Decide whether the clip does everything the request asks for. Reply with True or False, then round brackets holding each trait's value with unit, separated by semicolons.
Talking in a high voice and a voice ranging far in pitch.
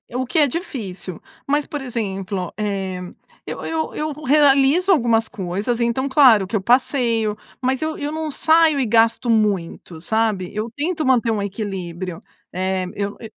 True (230 Hz; 5.9 semitones)